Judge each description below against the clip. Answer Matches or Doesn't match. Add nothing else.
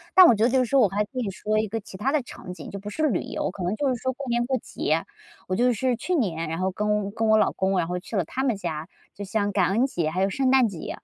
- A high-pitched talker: Matches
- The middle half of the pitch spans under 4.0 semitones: Doesn't match